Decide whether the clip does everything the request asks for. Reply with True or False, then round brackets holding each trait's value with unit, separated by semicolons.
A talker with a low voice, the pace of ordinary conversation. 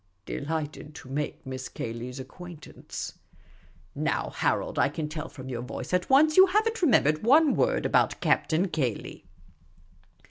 False (155 Hz; 165 wpm)